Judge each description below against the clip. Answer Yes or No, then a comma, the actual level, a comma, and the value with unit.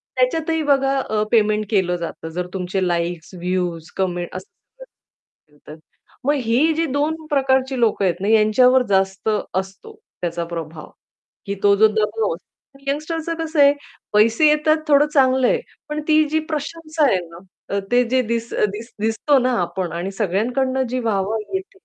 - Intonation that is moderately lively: No, wide, 7.1 semitones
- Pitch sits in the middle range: No, high, 225 Hz